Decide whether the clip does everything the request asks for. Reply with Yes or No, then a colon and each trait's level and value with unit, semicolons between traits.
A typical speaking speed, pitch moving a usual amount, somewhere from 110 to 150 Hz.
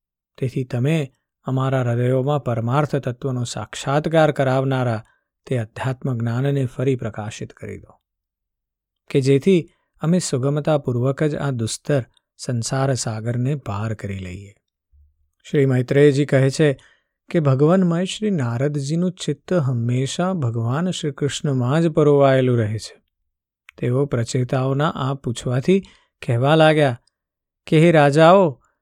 Yes: average, 110 wpm; average, 3.9 semitones; low, 135 Hz